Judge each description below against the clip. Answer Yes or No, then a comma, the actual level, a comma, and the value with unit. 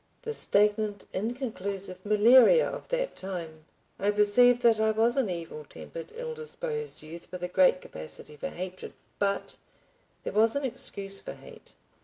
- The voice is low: No, high, 210 Hz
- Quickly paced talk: No, average, 155 wpm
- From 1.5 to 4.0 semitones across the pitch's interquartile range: No, average, 5.0 semitones